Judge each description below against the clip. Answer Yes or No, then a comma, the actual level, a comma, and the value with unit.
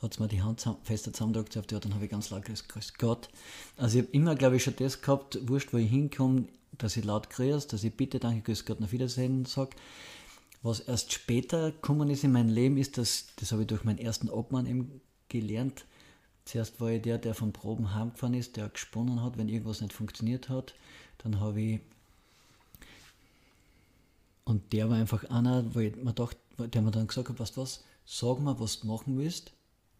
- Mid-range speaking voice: No, low, 115 Hz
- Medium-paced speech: No, fast, 205 wpm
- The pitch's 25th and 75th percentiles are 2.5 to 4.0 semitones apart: Yes, average, 2.8 semitones